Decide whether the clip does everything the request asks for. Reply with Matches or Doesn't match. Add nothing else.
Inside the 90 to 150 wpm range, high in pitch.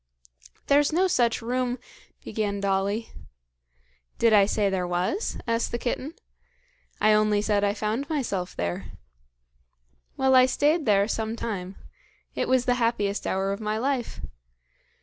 Matches